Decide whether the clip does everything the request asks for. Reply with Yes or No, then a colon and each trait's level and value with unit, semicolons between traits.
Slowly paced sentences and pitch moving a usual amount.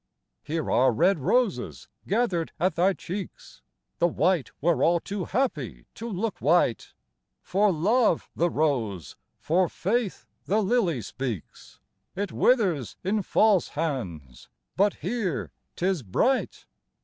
No: slow, 125 wpm; wide, 6.0 semitones